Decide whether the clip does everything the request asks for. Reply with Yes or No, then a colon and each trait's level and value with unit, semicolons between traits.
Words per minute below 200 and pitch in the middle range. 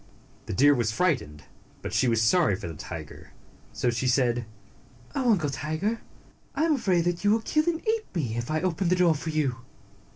No: fast, 205 wpm; medium, 155 Hz